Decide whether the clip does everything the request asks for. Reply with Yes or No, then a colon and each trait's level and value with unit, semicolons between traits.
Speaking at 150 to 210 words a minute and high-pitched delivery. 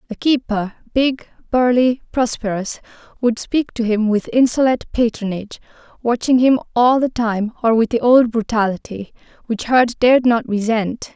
No: slow, 135 wpm; high, 235 Hz